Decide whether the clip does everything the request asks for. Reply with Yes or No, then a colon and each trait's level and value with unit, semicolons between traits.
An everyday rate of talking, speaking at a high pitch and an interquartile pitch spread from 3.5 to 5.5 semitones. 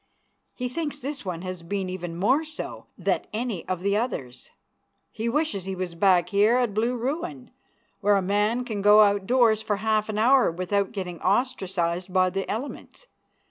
Yes: average, 180 wpm; high, 205 Hz; average, 4.7 semitones